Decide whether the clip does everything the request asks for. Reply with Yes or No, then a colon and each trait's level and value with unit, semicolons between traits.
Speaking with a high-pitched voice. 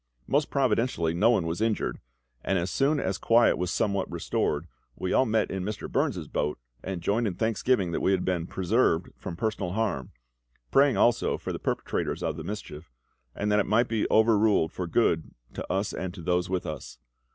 No: low, 100 Hz